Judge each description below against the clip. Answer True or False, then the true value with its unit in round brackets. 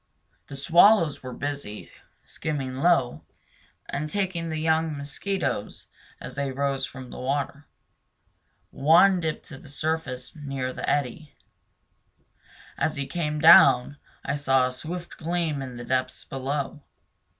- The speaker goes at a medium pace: False (130 wpm)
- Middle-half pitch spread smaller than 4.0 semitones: True (3.2 semitones)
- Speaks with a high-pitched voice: False (145 Hz)